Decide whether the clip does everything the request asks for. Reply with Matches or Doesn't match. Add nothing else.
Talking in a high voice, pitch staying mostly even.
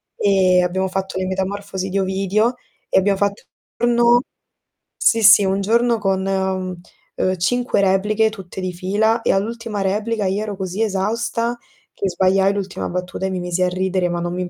Matches